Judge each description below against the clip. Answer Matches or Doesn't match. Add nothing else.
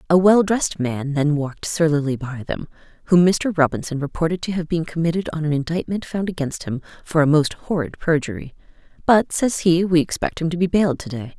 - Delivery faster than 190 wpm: Matches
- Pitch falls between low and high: Matches